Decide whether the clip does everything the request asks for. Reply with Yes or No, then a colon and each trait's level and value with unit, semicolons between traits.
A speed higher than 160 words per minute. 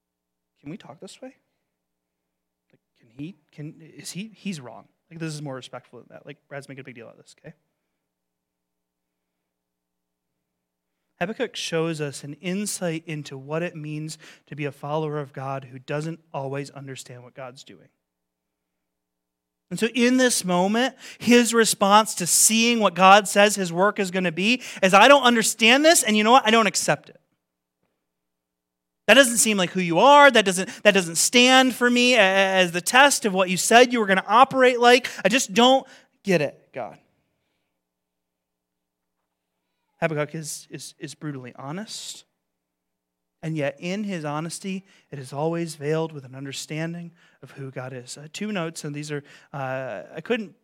Yes: average, 175 wpm